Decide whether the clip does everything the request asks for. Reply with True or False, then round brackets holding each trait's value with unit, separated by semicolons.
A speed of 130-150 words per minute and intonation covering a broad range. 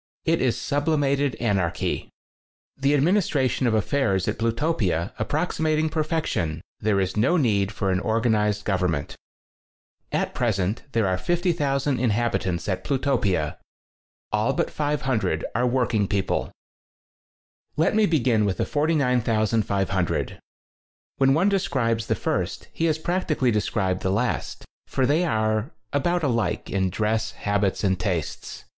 True (135 wpm; 6.3 semitones)